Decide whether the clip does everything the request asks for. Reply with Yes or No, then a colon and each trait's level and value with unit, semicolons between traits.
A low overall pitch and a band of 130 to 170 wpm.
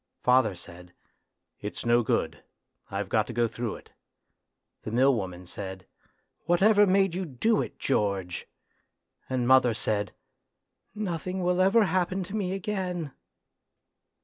Yes: low, 130 Hz; average, 145 wpm